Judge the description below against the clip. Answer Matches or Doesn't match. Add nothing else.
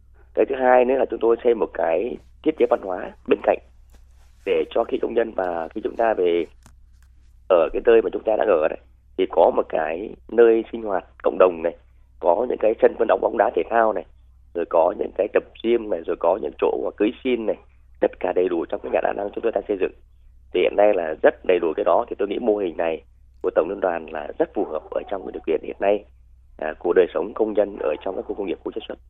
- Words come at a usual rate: Doesn't match